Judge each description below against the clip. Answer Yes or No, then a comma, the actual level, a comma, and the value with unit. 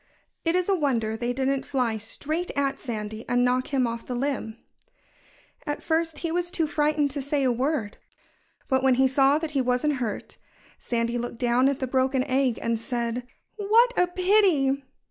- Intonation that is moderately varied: Yes, average, 3.8 semitones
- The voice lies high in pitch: Yes, very high, 265 Hz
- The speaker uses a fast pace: No, average, 185 wpm